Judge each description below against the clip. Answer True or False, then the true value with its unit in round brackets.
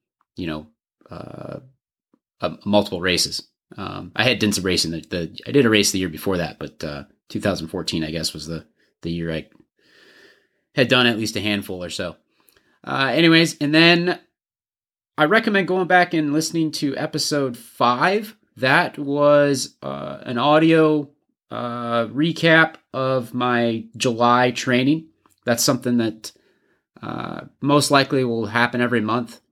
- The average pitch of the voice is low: True (125 Hz)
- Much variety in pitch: True (6.4 semitones)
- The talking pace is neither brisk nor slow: True (150 wpm)